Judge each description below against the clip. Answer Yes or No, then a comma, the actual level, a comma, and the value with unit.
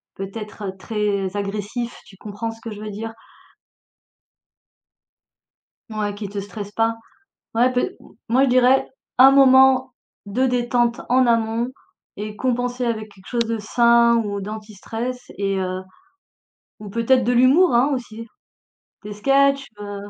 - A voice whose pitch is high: Yes, high, 225 Hz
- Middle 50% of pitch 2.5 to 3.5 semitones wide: Yes, average, 3.2 semitones